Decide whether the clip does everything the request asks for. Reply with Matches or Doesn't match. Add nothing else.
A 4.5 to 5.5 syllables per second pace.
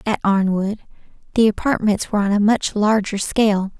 Matches